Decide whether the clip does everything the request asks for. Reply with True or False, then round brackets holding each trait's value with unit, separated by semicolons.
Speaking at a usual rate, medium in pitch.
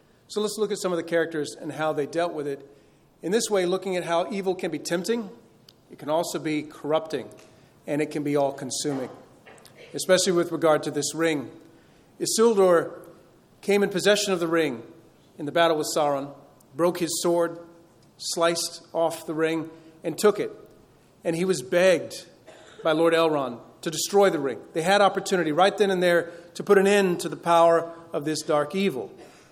True (185 wpm; 170 Hz)